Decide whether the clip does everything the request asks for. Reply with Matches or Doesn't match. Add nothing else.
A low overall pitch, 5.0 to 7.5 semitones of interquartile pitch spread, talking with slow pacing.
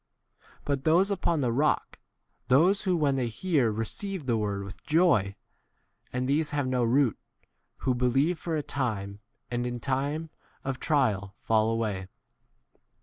Doesn't match